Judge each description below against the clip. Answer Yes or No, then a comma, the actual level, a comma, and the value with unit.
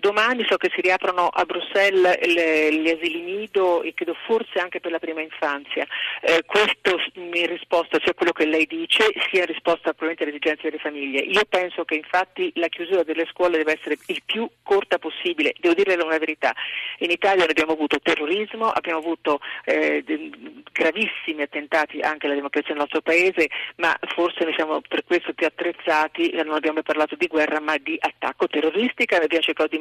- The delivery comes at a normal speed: No, fast, 180 wpm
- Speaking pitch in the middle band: Yes, medium, 165 Hz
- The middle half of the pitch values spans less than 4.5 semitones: Yes, average, 3.1 semitones